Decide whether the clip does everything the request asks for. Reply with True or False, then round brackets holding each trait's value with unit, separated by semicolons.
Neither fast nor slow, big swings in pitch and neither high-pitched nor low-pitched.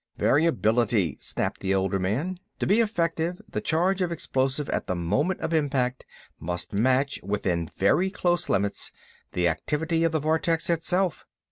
True (150 wpm; 9.0 semitones; 145 Hz)